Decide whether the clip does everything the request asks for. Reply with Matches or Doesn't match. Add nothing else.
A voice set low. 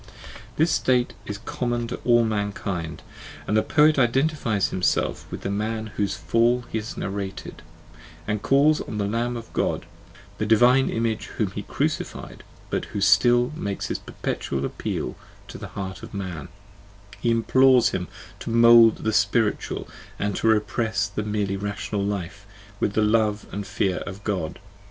Matches